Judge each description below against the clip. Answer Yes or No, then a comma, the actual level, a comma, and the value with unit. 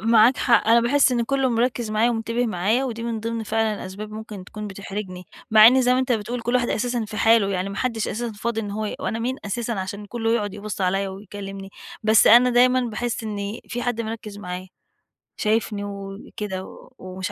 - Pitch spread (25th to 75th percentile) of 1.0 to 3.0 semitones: Yes, average, 2.7 semitones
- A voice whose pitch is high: Yes, high, 220 Hz